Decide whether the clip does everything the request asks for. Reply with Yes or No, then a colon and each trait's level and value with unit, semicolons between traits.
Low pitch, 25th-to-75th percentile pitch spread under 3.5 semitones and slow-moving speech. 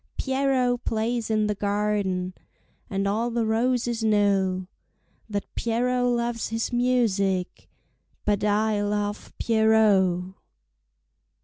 No: high, 220 Hz; average, 2.7 semitones; slow, 100 wpm